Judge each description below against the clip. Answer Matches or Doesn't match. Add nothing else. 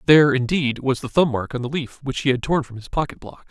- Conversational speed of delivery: Doesn't match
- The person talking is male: Matches